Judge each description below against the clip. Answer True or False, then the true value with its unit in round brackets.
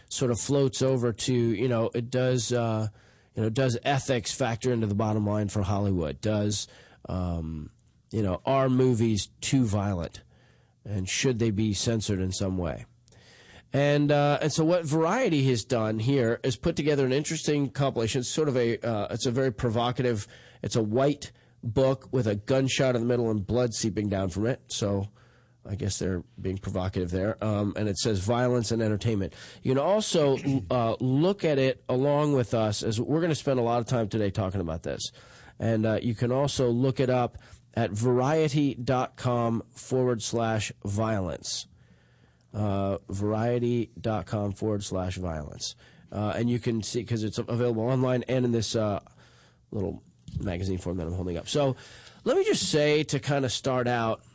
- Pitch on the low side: True (120 Hz)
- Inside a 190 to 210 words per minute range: False (180 wpm)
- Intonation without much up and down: False (3.9 semitones)